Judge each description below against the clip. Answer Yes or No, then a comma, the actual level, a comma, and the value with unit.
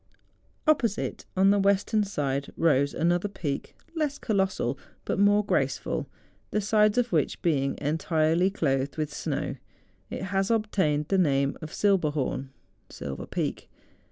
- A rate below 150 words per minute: Yes, slow, 135 wpm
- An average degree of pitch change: No, wide, 5.7 semitones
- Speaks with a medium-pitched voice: Yes, medium, 175 Hz